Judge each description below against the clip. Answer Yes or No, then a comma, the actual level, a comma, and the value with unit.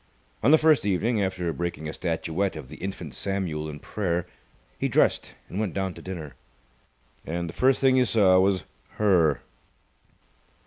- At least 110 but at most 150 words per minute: No, average, 165 wpm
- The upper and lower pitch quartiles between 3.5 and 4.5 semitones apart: Yes, average, 3.8 semitones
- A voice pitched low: Yes, very low, 95 Hz